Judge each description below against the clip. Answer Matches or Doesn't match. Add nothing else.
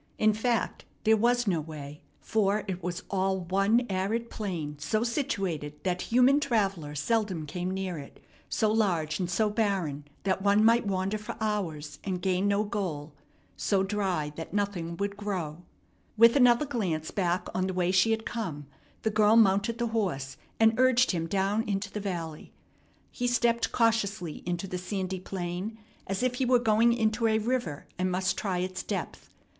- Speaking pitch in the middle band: Doesn't match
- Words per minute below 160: Doesn't match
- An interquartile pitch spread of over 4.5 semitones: Doesn't match